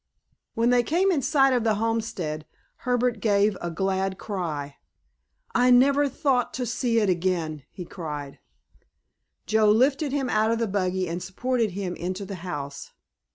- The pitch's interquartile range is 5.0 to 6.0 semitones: Yes, wide, 5.4 semitones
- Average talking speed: Yes, average, 155 wpm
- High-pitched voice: Yes, high, 210 Hz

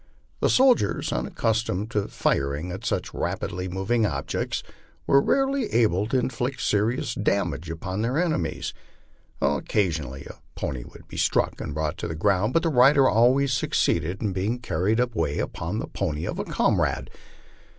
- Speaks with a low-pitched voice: Yes, low, 105 Hz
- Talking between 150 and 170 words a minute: Yes, average, 160 wpm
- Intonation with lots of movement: Yes, wide, 6.8 semitones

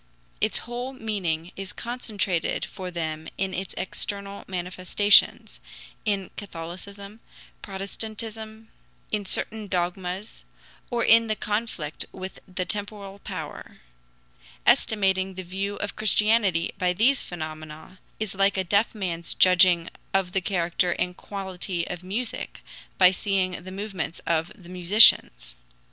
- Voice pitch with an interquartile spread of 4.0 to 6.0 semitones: No, average, 2.8 semitones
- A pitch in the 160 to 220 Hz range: Yes, high, 190 Hz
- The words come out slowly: Yes, slow, 125 wpm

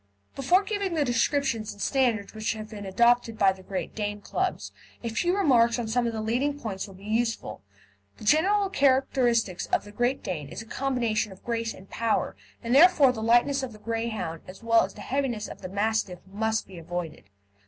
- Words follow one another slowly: No, average, 200 wpm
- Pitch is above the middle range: Yes, high, 230 Hz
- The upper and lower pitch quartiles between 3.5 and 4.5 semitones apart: Yes, average, 4.2 semitones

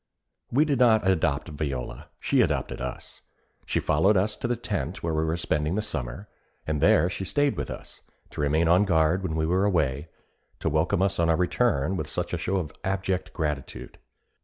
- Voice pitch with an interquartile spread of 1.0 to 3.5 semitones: No, average, 4.1 semitones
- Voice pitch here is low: Yes, very low, 85 Hz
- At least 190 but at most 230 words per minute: Yes, average, 195 wpm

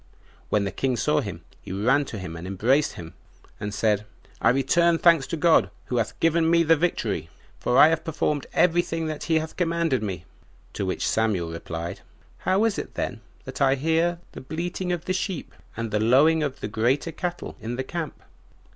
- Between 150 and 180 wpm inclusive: No, average, 200 wpm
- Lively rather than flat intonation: Yes, wide, 7.3 semitones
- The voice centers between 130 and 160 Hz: Yes, medium, 140 Hz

